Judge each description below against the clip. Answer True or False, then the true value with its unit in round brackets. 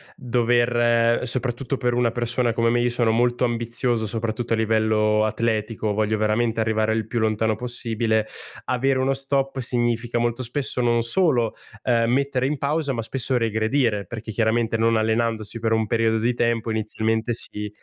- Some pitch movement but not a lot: False (1.7 semitones)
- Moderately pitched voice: False (115 Hz)